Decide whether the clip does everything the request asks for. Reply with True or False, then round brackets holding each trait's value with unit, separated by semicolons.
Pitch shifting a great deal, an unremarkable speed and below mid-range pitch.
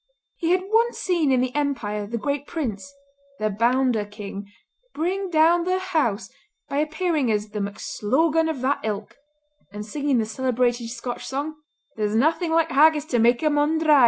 False (6.1 semitones; 160 wpm; 280 Hz)